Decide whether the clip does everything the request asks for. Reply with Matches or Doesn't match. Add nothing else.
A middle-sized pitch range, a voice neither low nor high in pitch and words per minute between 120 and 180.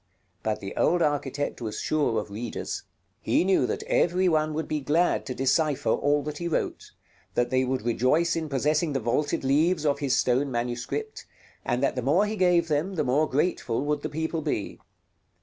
Doesn't match